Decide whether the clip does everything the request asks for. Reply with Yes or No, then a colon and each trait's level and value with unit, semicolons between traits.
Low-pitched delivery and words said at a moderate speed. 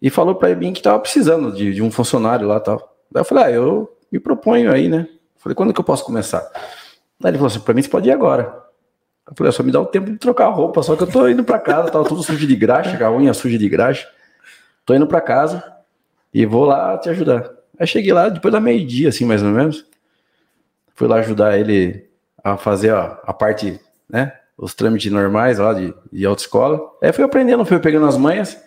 No: low, 130 Hz; fast, 230 wpm